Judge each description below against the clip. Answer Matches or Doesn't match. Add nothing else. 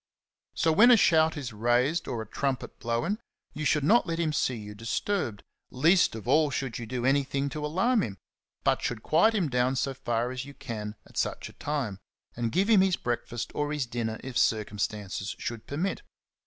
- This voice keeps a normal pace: Matches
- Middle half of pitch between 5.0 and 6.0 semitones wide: Matches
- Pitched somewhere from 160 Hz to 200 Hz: Doesn't match